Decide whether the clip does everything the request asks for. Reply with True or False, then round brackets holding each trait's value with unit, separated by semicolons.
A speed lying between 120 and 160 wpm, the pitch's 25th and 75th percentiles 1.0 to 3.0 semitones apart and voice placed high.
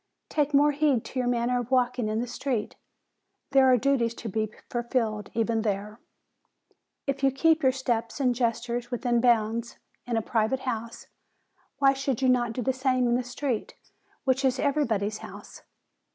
False (170 wpm; 2.5 semitones; 245 Hz)